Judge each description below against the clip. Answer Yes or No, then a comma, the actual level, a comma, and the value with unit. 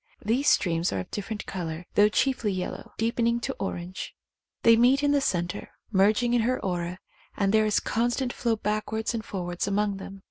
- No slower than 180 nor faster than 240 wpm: Yes, average, 200 wpm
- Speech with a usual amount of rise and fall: Yes, average, 4.0 semitones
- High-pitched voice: Yes, high, 210 Hz